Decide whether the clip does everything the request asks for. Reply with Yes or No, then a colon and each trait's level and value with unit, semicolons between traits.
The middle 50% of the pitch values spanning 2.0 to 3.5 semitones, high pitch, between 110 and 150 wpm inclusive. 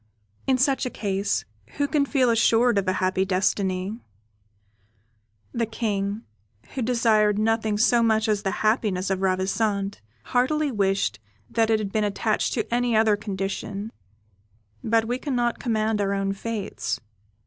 Yes: average, 3.0 semitones; high, 215 Hz; average, 145 wpm